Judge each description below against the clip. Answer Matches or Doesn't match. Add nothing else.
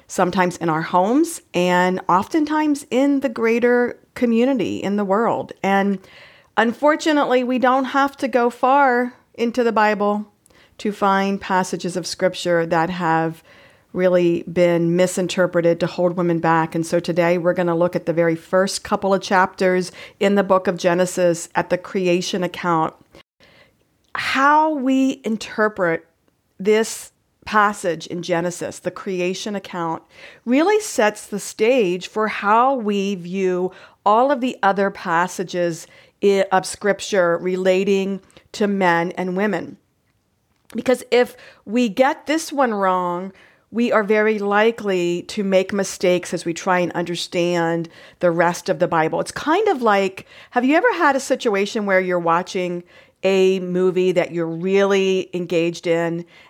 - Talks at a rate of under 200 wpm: Matches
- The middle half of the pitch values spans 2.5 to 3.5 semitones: Doesn't match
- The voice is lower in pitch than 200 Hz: Matches